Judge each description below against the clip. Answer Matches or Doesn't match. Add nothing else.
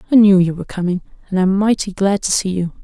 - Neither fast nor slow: Doesn't match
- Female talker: Matches